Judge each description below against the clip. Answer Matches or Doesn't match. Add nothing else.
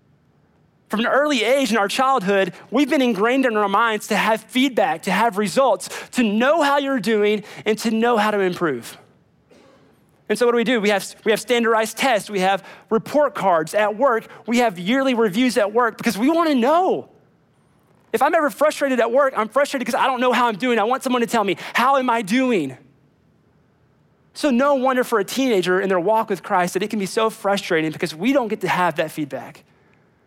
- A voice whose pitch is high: Matches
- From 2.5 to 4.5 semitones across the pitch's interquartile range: Doesn't match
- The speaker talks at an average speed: Doesn't match